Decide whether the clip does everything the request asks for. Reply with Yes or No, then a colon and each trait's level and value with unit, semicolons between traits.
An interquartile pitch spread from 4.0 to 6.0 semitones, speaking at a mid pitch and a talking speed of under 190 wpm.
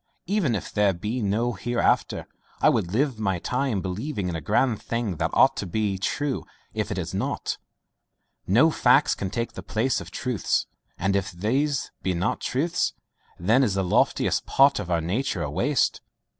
No: wide, 5.6 semitones; low, 110 Hz; average, 180 wpm